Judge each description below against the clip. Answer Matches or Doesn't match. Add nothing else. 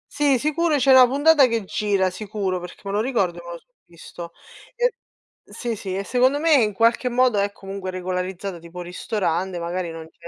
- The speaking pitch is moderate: Doesn't match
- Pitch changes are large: Matches